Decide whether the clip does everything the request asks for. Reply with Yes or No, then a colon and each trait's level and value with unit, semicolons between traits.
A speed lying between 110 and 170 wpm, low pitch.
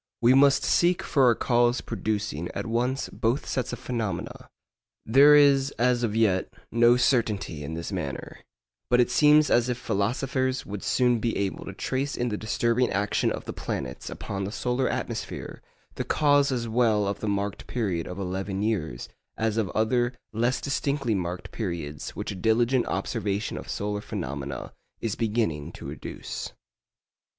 Yes: average, 160 wpm; low, 115 Hz